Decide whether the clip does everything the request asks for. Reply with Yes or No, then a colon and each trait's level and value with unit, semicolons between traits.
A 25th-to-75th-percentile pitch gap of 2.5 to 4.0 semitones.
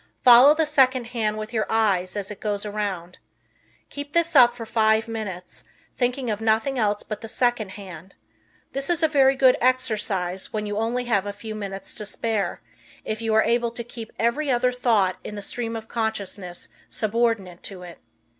Yes: average, 3.1 semitones